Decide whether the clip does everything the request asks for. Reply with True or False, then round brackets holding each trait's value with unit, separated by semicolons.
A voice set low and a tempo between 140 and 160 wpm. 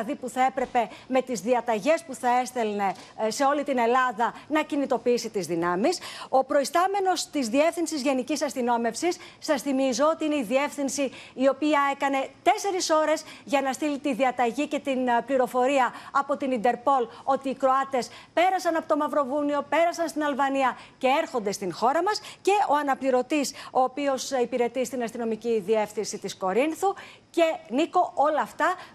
False (270 Hz; 155 wpm)